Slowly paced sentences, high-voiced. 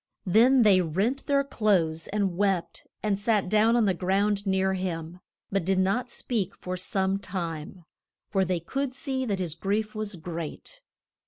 No: average, 165 wpm; high, 195 Hz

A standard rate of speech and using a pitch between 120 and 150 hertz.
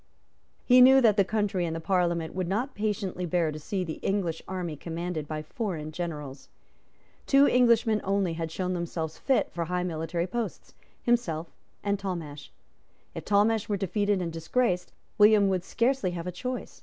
No: average, 170 wpm; medium, 185 Hz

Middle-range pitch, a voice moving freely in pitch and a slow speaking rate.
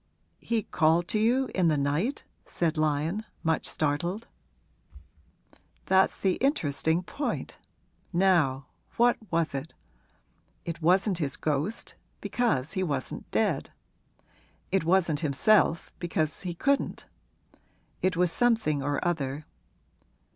No: medium, 170 Hz; average, 4.2 semitones; slow, 110 wpm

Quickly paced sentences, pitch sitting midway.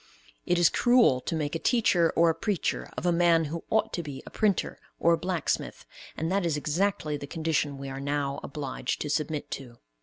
Yes: fast, 210 wpm; medium, 160 Hz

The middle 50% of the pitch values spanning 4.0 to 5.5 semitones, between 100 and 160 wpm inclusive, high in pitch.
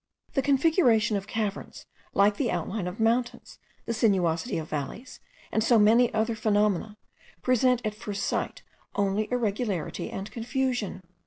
No: average, 3.3 semitones; average, 140 wpm; high, 220 Hz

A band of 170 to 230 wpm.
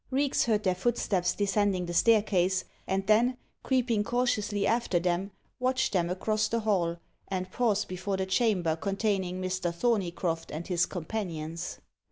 No: average, 145 wpm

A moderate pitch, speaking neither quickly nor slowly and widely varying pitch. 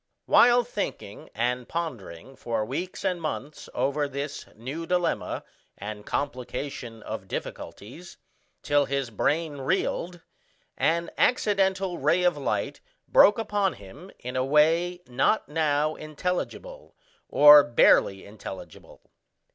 No: medium, 150 Hz; slow, 115 wpm; wide, 5.9 semitones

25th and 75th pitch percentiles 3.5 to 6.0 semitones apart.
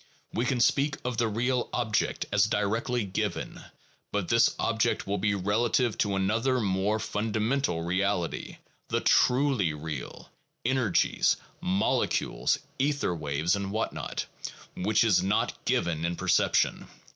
Yes: average, 4.3 semitones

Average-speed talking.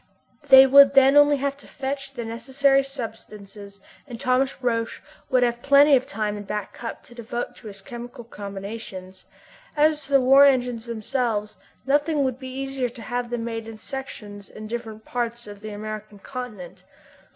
Yes: average, 175 wpm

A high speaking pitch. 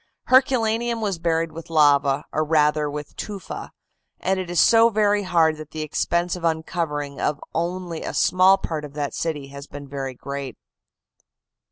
No: medium, 160 Hz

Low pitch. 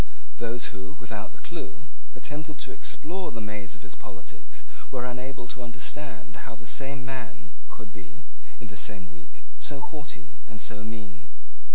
Yes: low, 115 Hz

